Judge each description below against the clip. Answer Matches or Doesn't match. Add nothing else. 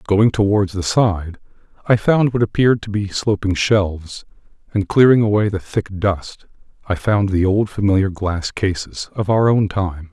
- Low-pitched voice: Matches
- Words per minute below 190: Matches